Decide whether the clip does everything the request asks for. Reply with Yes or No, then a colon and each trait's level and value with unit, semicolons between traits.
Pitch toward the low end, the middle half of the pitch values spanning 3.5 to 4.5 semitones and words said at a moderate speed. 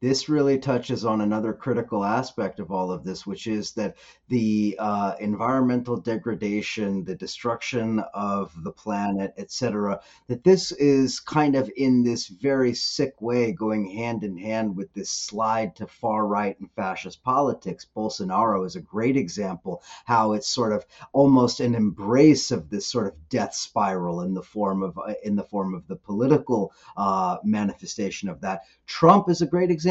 Yes: low, 110 Hz; average, 3.9 semitones; average, 175 wpm